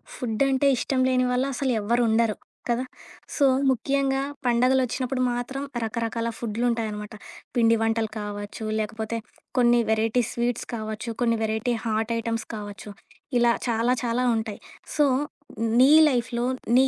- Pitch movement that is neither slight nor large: No, narrow, 2.3 semitones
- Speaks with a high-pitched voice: Yes, high, 235 Hz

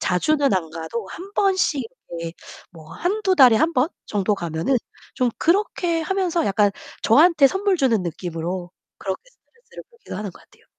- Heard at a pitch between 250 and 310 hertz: Yes, very high, 255 Hz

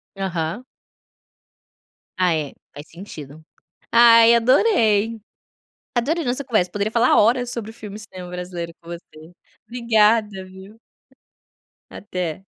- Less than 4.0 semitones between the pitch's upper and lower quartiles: No, average, 4.6 semitones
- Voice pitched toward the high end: Yes, high, 210 Hz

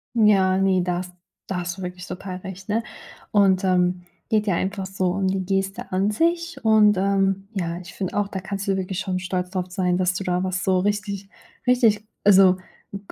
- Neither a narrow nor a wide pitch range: No, narrow, 1.7 semitones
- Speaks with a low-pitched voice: No, high, 190 Hz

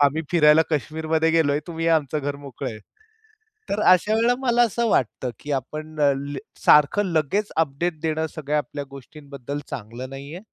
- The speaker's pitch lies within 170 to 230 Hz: No, medium, 150 Hz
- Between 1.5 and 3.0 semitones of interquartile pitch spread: Yes, narrow, 2.6 semitones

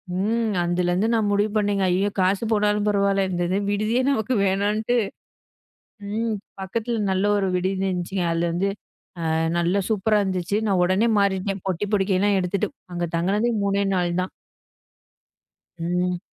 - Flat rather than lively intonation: Yes, narrow, 2.3 semitones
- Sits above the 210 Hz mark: No, high, 195 Hz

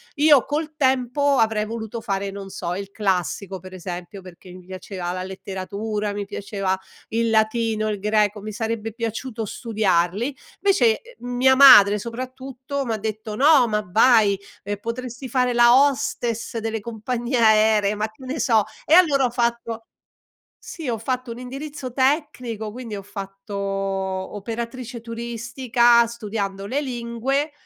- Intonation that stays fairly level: No, average, 3.7 semitones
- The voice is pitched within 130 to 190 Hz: No, high, 225 Hz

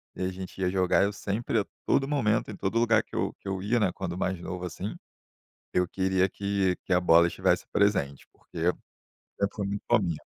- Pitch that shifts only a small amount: Yes, narrow, 2.3 semitones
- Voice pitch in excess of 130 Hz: No, very low, 95 Hz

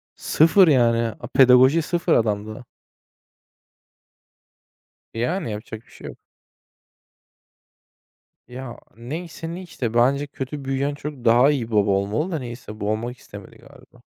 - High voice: No, low, 125 Hz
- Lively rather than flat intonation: No, average, 4.6 semitones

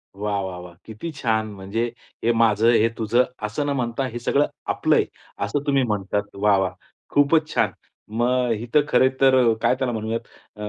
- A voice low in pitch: Yes, low, 115 Hz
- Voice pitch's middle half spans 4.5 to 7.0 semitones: No, average, 3.5 semitones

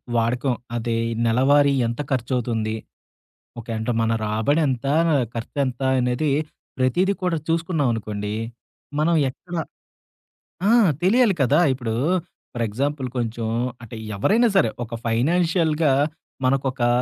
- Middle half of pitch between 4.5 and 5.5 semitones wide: Yes, average, 4.8 semitones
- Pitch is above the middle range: No, low, 130 Hz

